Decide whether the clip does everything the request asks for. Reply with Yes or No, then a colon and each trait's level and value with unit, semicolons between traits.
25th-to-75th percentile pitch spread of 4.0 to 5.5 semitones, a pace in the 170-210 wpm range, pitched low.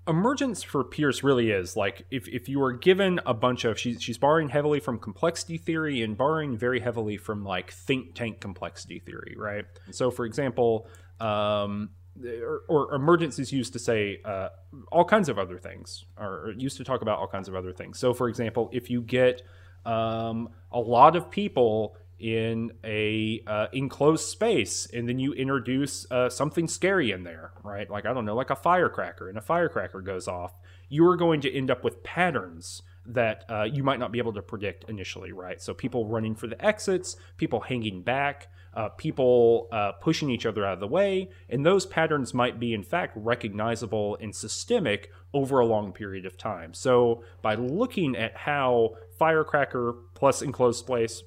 Yes: average, 5.0 semitones; average, 185 wpm; low, 115 Hz